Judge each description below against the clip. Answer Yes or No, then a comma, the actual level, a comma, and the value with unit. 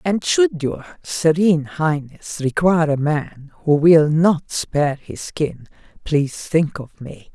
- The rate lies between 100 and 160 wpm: Yes, average, 145 wpm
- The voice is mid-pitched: Yes, medium, 155 Hz